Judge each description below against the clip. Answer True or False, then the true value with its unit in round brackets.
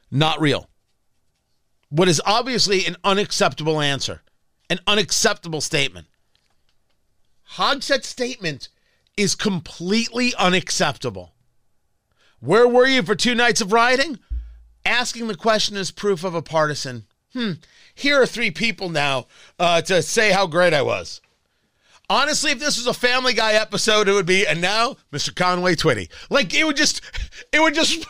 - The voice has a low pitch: False (195 Hz)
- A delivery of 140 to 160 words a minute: True (145 wpm)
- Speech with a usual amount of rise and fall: False (6.8 semitones)